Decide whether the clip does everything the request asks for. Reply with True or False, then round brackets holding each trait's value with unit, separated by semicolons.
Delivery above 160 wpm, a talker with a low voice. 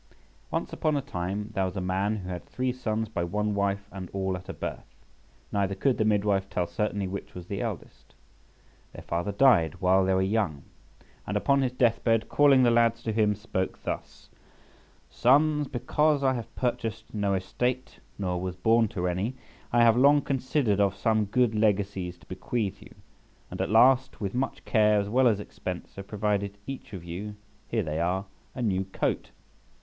True (185 wpm; 105 Hz)